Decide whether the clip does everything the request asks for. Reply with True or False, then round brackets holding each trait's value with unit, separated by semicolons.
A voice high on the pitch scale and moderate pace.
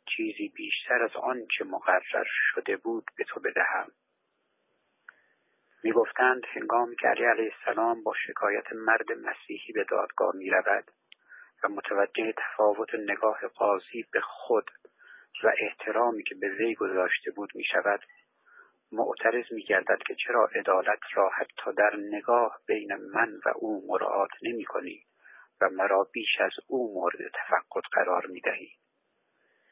True (340 Hz; 135 wpm)